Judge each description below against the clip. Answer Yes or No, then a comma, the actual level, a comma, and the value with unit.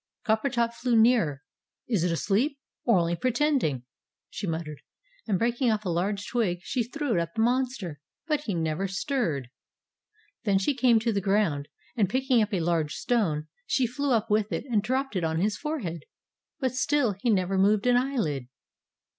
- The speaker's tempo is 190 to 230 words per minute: No, average, 180 wpm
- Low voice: No, high, 215 Hz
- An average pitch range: No, wide, 6.3 semitones